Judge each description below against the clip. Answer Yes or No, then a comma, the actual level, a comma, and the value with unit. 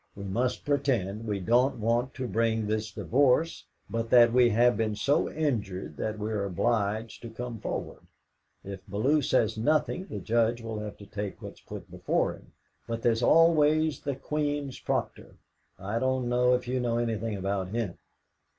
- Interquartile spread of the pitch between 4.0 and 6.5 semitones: No, average, 3.2 semitones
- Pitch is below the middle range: Yes, low, 115 Hz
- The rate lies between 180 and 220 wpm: No, average, 170 wpm